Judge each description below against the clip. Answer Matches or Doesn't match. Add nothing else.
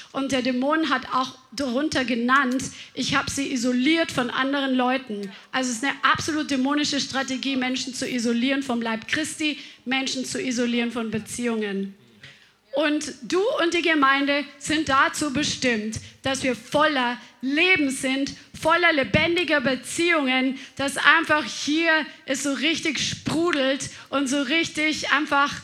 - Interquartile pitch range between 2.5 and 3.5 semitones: Matches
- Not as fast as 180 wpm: Matches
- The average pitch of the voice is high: Matches